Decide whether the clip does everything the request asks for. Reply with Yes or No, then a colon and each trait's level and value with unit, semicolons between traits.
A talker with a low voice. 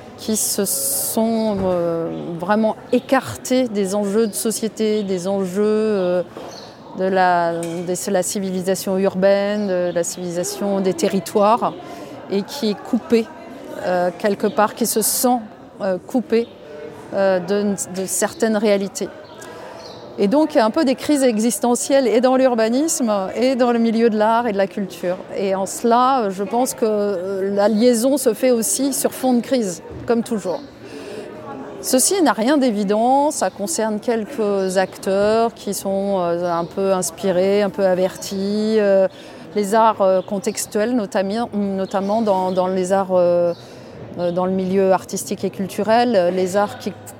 No: high, 205 Hz